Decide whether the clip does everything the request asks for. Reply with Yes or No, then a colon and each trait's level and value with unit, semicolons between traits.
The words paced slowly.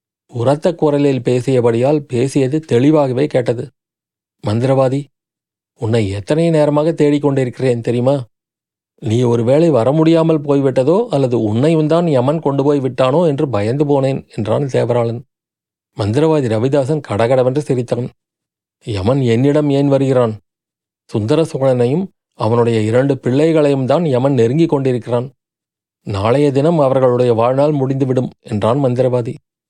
No: average, 105 wpm